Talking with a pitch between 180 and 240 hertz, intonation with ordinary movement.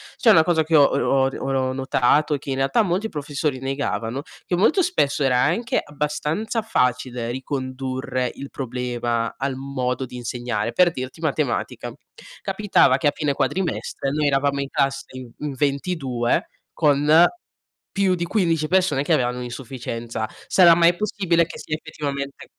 No: medium, 140 Hz; average, 4.1 semitones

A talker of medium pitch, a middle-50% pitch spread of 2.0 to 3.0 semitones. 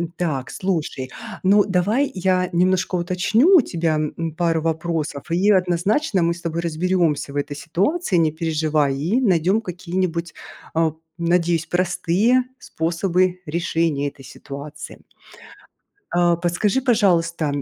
Yes: medium, 170 Hz; narrow, 2.5 semitones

